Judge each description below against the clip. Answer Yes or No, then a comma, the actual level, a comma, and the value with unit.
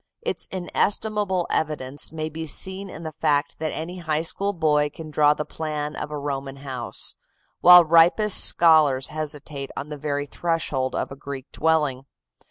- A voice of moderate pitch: Yes, medium, 155 Hz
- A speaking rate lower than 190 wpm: Yes, average, 165 wpm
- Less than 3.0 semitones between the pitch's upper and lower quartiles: Yes, narrow, 2.6 semitones